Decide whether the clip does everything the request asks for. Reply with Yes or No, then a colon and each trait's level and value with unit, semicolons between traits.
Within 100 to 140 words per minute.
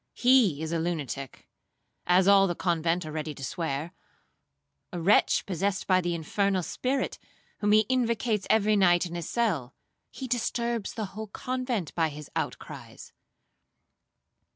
Yes: slow, 135 wpm